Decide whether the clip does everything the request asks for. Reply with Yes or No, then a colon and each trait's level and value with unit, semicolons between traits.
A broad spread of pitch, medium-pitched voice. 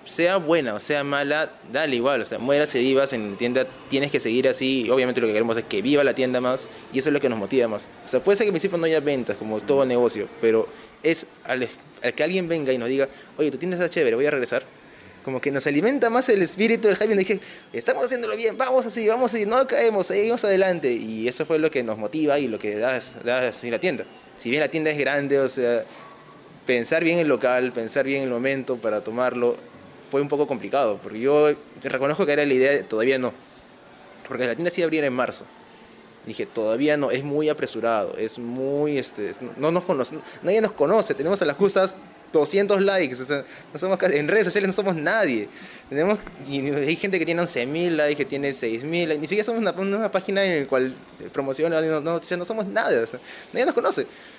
Yes: wide, 6.2 semitones; medium, 145 Hz